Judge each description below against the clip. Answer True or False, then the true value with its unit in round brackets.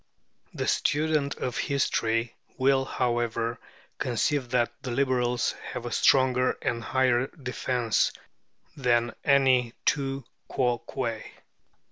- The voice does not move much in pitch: True (2.1 semitones)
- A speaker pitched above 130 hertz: False (125 Hz)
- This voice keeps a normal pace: False (100 wpm)